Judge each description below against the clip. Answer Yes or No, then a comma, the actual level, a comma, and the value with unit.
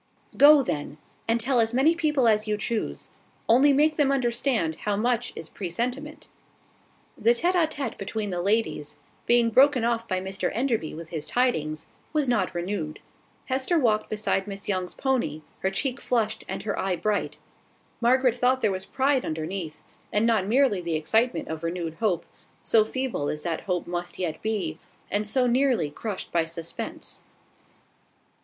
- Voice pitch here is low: No, high, 220 Hz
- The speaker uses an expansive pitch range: Yes, wide, 6.0 semitones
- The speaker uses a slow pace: No, average, 165 wpm